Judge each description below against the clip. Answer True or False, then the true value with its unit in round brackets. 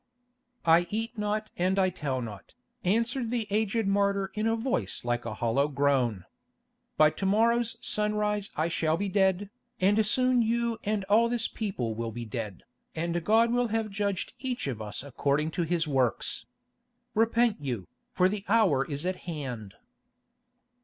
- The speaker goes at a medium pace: True (160 wpm)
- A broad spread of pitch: True (7.5 semitones)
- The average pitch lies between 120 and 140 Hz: False (195 Hz)